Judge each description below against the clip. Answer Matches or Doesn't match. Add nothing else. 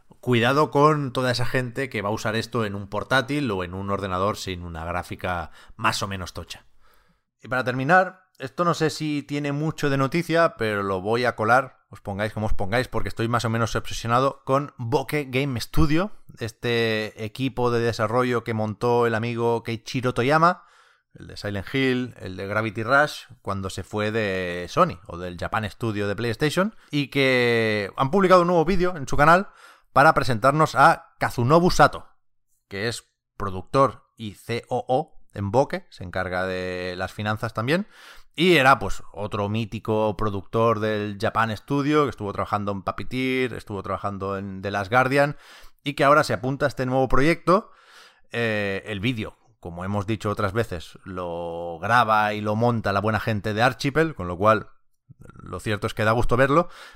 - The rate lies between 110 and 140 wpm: Doesn't match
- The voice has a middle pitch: Doesn't match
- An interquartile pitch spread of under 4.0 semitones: Doesn't match